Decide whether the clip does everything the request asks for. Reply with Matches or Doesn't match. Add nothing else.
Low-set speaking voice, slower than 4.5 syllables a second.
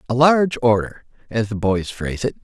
Doesn't match